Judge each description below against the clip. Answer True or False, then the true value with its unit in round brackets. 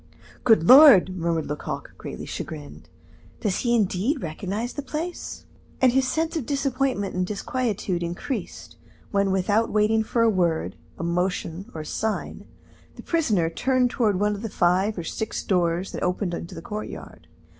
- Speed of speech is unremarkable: True (160 wpm)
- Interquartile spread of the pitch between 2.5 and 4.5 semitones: False (5.6 semitones)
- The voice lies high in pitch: True (205 Hz)